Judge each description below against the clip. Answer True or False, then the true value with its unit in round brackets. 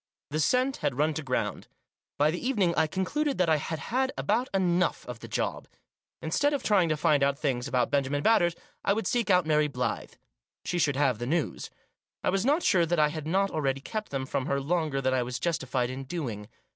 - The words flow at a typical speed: False (220 wpm)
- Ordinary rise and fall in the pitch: False (5.7 semitones)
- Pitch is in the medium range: True (155 Hz)